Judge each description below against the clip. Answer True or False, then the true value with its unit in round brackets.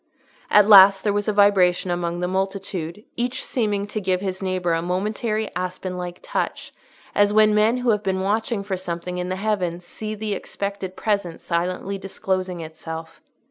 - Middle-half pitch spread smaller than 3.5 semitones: True (2.5 semitones)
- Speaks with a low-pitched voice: False (190 Hz)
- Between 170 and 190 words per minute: True (175 wpm)